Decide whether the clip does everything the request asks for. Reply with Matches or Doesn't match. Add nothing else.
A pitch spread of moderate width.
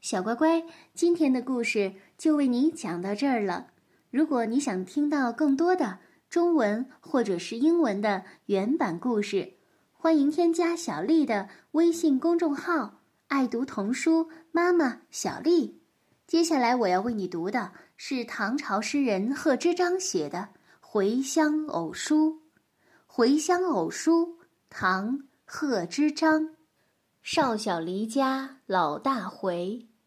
Doesn't match